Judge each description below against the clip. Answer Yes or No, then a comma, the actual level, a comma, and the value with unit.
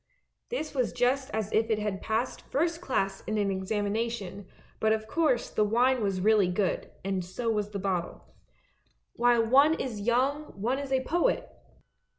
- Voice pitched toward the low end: No, high, 220 Hz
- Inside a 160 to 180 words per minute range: Yes, average, 165 wpm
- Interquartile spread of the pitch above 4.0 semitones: Yes, average, 4.4 semitones